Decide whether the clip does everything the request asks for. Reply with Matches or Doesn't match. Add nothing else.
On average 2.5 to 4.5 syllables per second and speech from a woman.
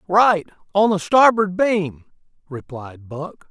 Doesn't match